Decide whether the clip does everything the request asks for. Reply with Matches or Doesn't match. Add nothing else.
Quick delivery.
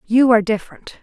Doesn't match